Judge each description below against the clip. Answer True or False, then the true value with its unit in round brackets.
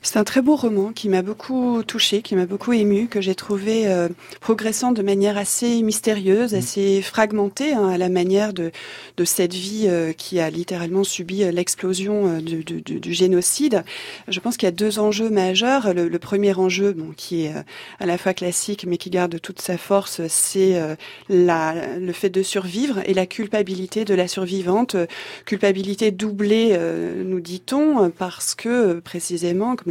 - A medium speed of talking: True (185 wpm)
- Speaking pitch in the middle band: False (195 Hz)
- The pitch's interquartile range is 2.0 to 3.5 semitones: True (2.9 semitones)